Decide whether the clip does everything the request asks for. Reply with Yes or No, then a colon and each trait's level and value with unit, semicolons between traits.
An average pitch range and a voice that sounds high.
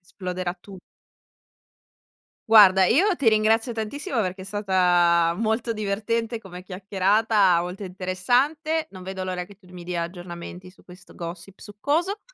Yes: average, 3.6 semitones; high, 195 Hz